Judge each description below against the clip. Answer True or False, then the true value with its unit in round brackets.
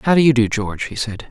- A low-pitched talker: True (120 Hz)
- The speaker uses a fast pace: True (320 wpm)